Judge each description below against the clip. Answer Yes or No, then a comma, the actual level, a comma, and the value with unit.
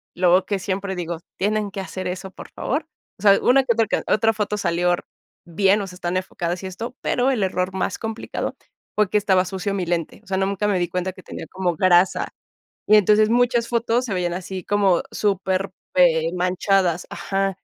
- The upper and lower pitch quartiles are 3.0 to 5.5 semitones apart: No, narrow, 2.5 semitones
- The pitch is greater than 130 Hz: Yes, high, 190 Hz